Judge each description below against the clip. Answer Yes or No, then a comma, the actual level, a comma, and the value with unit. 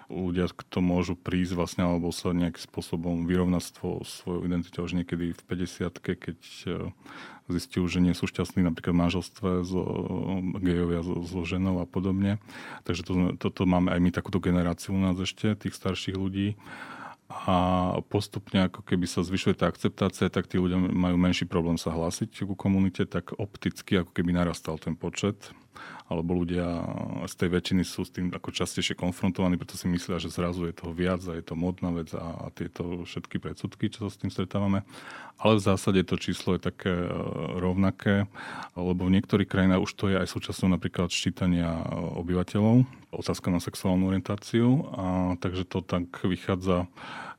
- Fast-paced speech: Yes, fast, 175 wpm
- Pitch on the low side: Yes, very low, 90 Hz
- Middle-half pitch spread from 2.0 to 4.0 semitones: No, narrow, 1.6 semitones